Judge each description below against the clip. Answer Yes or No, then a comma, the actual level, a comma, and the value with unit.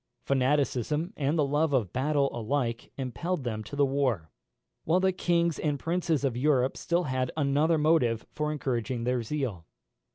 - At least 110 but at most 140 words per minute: No, average, 160 wpm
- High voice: No, medium, 140 Hz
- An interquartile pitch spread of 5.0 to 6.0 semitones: No, average, 3.8 semitones